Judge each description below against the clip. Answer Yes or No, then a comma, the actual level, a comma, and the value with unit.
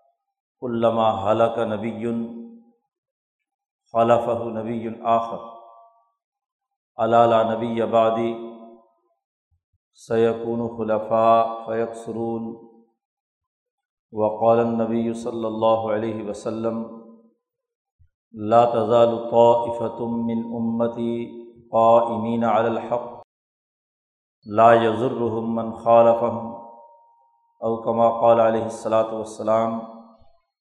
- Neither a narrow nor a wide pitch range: No, narrow, 0.7 semitones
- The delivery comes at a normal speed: No, slow, 60 wpm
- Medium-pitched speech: No, low, 115 Hz